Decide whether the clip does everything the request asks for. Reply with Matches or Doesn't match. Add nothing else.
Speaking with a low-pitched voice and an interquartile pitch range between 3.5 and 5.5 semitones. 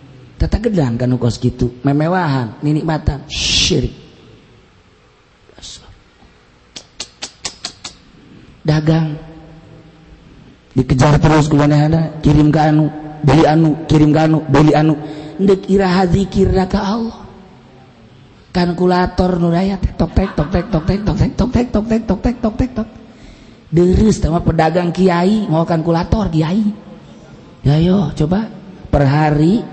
Doesn't match